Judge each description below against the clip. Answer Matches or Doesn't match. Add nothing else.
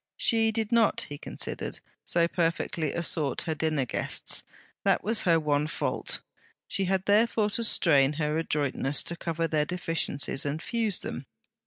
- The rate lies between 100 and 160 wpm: Matches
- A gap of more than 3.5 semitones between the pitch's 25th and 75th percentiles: Matches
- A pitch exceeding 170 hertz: Doesn't match